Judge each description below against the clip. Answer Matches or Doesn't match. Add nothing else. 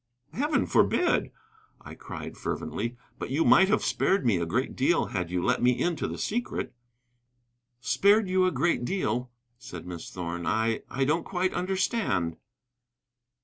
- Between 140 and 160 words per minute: Matches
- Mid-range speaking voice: Doesn't match